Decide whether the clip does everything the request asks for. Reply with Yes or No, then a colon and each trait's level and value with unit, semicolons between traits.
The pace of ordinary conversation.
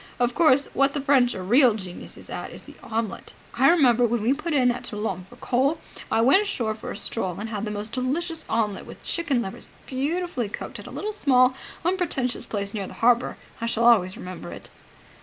No: fast, 210 wpm